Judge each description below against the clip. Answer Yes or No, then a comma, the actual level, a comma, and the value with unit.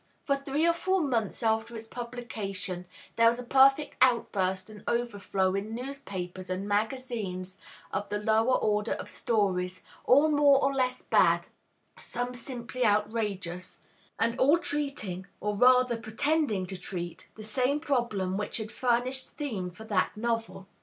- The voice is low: No, high, 225 Hz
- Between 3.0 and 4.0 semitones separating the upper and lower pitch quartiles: No, average, 4.4 semitones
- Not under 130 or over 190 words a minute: Yes, average, 145 wpm